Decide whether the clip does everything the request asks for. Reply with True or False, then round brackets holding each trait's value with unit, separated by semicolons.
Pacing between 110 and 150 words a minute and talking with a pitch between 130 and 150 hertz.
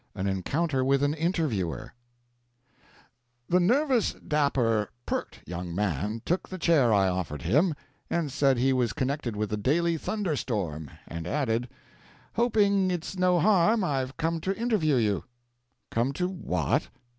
True (140 wpm; 140 Hz)